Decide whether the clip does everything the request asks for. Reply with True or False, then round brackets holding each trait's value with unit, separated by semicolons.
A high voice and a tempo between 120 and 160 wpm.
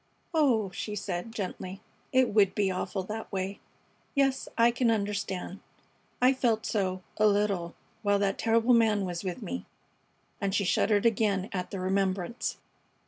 True (205 Hz; 150 wpm)